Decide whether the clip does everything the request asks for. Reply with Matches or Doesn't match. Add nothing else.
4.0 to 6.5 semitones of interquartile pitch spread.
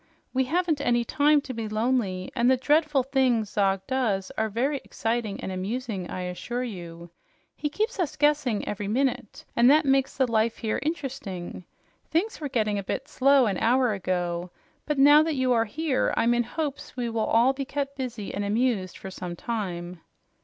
Matches